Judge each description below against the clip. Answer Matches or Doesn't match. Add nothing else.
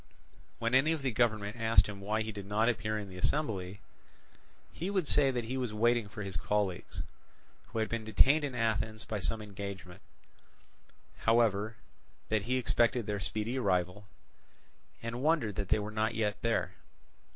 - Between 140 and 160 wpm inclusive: Doesn't match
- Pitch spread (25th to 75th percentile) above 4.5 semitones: Doesn't match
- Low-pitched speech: Matches